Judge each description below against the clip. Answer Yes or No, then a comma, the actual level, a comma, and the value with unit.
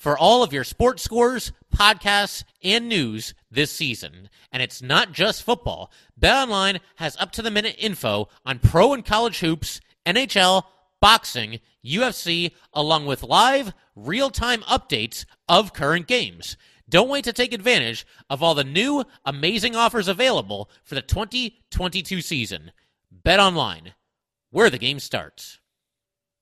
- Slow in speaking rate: Yes, slow, 130 wpm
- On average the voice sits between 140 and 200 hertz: Yes, medium, 185 Hz